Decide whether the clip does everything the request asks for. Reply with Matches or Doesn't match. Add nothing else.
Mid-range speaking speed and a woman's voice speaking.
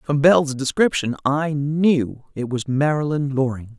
Matches